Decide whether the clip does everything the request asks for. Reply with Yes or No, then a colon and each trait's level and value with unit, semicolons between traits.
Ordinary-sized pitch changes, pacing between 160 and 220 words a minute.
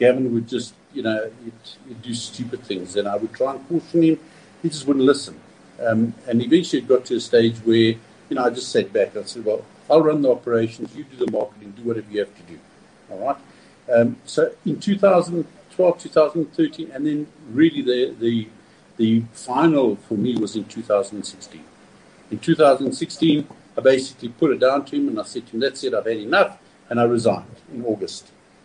No: wide, 7.4 semitones; average, 200 wpm